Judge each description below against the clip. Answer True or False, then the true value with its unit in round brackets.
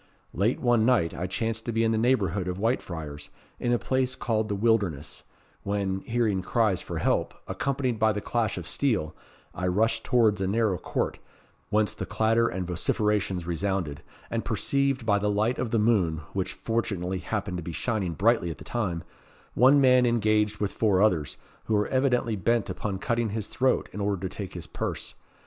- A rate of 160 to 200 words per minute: True (185 wpm)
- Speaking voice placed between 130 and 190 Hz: False (105 Hz)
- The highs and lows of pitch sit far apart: False (3.8 semitones)